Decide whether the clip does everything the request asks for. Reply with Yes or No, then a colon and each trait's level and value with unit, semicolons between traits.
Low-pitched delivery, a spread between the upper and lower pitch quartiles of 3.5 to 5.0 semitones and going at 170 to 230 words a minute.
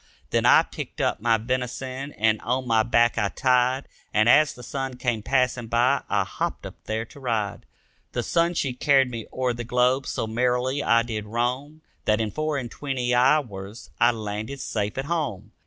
No: low, 125 Hz; average, 2.9 semitones; average, 190 wpm